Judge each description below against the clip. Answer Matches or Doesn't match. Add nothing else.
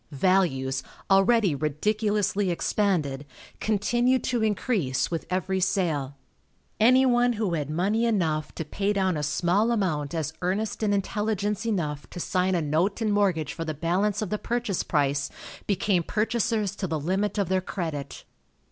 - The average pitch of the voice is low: Doesn't match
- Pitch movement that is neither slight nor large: Matches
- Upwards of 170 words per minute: Doesn't match